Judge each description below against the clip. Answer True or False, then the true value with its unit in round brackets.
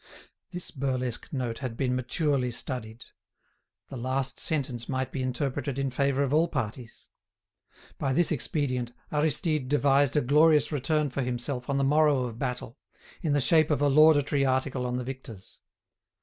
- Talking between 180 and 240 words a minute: False (160 wpm)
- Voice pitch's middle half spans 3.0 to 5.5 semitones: False (2.6 semitones)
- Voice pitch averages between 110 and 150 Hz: True (135 Hz)